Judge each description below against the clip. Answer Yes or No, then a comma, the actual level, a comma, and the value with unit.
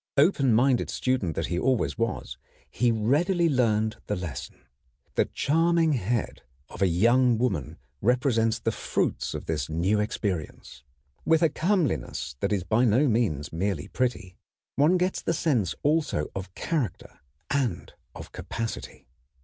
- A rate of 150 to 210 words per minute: No, average, 140 wpm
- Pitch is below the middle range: Yes, low, 115 Hz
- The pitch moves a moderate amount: No, wide, 7.0 semitones